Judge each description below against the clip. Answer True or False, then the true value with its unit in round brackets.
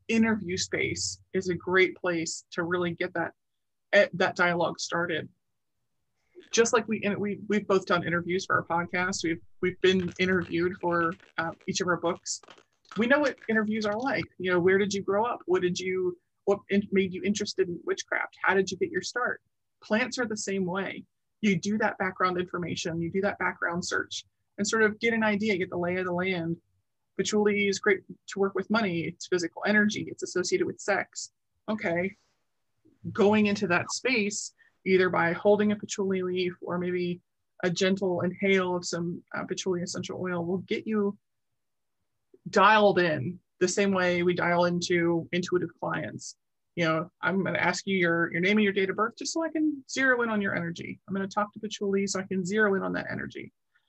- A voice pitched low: False (190 Hz)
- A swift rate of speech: False (195 wpm)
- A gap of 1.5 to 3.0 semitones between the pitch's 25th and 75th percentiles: True (2.7 semitones)